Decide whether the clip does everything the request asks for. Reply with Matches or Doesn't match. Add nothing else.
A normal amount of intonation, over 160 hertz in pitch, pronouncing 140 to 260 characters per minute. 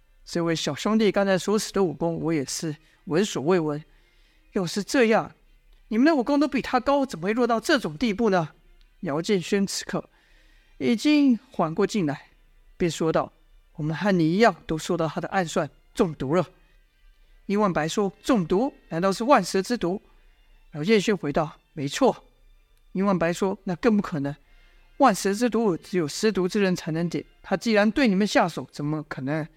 Matches